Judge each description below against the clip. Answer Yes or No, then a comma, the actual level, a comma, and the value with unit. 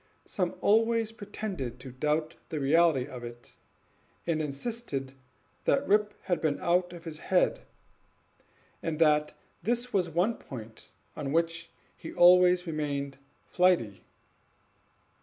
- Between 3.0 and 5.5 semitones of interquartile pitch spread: Yes, average, 4.4 semitones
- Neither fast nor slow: No, slow, 120 wpm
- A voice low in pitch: No, medium, 165 Hz